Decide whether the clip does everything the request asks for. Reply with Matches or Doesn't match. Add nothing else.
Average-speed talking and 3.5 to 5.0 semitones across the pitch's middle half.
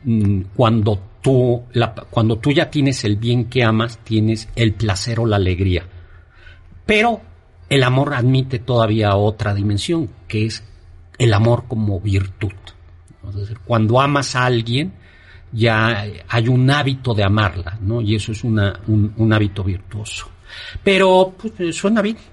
Matches